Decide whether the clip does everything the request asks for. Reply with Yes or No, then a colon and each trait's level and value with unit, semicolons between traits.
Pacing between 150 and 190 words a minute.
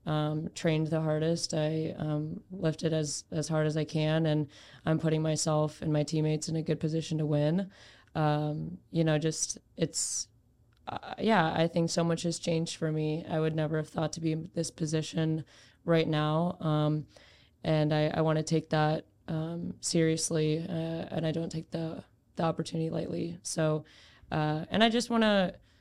Yes: average, 185 wpm